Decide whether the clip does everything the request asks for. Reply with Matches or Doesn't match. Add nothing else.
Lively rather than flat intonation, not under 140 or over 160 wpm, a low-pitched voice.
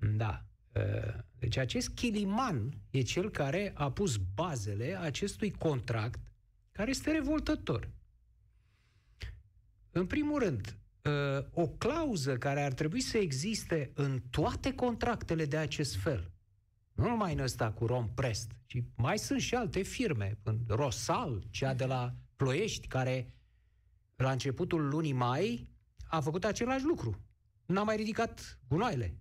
Doesn't match